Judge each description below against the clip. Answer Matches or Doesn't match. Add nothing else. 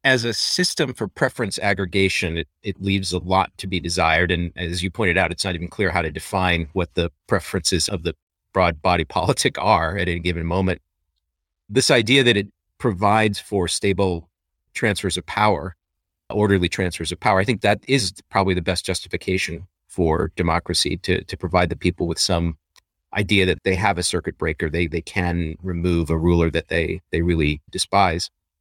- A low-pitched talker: Matches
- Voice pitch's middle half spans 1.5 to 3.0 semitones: Matches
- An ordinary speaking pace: Matches